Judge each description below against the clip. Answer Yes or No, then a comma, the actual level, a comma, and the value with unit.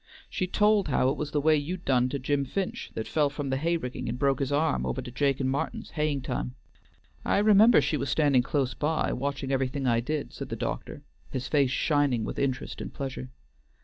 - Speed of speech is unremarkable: No, fast, 215 wpm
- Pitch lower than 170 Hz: Yes, medium, 140 Hz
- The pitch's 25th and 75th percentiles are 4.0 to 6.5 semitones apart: No, average, 2.8 semitones